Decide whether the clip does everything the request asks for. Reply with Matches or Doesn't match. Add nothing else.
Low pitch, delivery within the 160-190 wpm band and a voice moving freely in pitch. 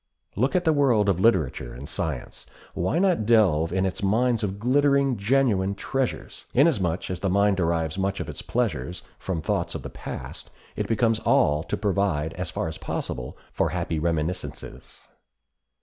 Matches